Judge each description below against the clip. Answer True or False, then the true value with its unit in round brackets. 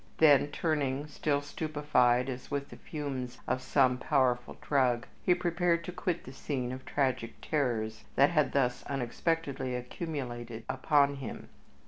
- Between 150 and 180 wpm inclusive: False (140 wpm)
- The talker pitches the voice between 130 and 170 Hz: True (135 Hz)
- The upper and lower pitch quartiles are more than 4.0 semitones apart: False (3.3 semitones)